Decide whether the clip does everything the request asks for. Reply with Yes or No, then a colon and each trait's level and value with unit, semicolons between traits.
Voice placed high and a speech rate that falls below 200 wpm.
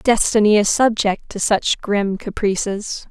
Yes: high, 210 Hz; slow, 135 wpm